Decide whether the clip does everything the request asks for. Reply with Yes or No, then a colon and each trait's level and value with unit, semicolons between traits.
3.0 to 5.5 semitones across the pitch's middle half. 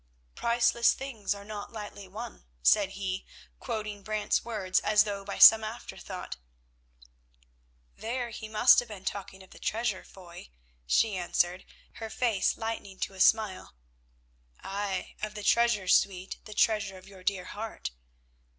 No: narrow, 2.5 semitones